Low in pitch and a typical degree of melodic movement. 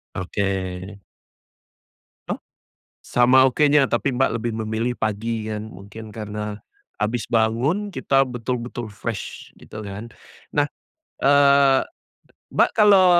Yes: low, 120 Hz; average, 4.0 semitones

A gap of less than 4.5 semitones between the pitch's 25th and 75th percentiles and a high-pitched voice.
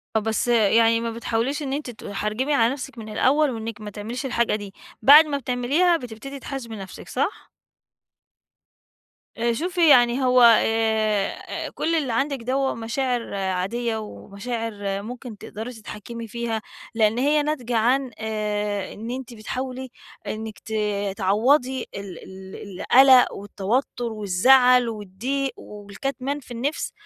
Yes: average, 3.7 semitones; high, 235 Hz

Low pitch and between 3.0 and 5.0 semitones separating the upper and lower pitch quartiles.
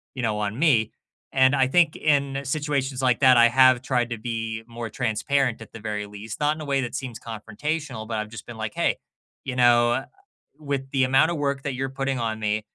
Yes: low, 125 Hz; average, 3.5 semitones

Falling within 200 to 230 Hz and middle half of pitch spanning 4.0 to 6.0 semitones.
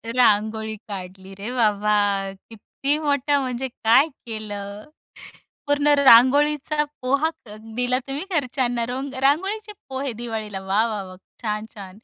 No: high, 240 Hz; average, 4.9 semitones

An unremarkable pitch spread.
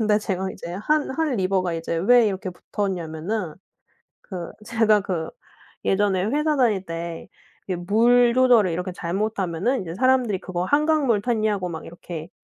Yes: average, 4.9 semitones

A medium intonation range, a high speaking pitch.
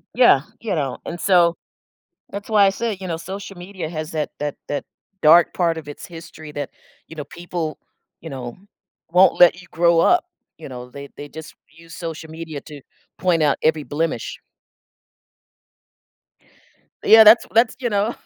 No: average, 3.7 semitones; medium, 165 Hz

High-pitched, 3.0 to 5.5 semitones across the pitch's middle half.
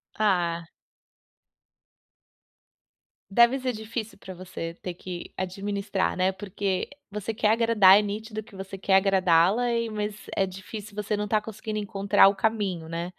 No: high, 200 Hz; narrow, 2.4 semitones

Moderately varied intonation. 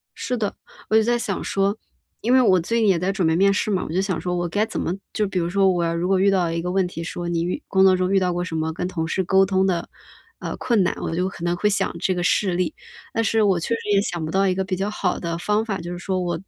No: narrow, 2.2 semitones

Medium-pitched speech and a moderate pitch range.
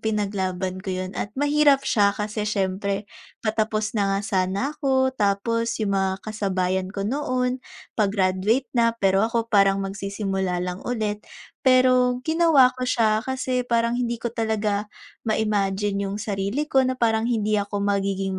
No: high, 210 Hz; average, 3.6 semitones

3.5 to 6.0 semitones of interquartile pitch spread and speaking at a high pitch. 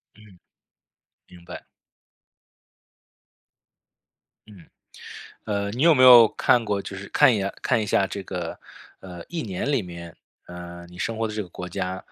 No: average, 4.0 semitones; low, 100 Hz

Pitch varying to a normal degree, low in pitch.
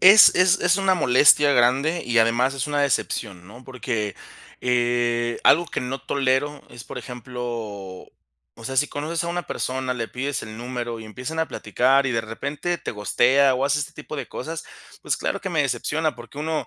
Yes: average, 3.7 semitones; low, 130 Hz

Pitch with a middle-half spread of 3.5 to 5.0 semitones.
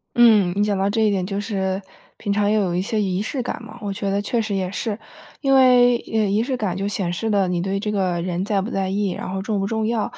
No: narrow, 2.4 semitones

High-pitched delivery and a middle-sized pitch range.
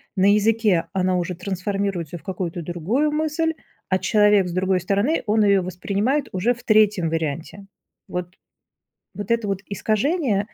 Yes: high, 200 Hz; average, 3.1 semitones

